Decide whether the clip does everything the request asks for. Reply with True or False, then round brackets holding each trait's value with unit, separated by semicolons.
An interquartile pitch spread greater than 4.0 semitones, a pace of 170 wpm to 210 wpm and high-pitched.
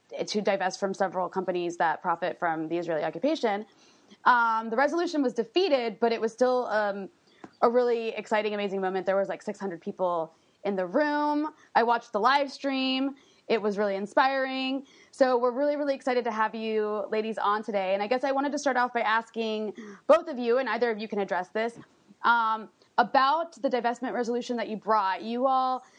True (4.5 semitones; 195 wpm; 225 Hz)